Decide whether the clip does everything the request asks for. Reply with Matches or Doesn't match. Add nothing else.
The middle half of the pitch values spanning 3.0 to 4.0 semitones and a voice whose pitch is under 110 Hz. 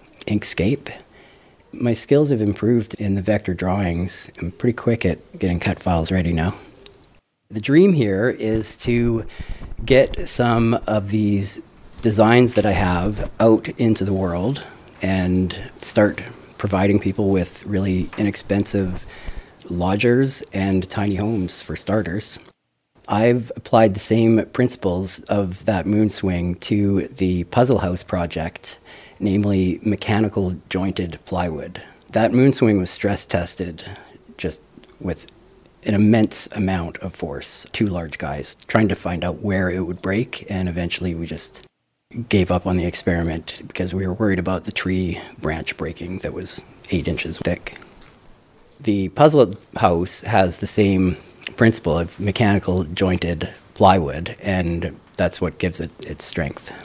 Matches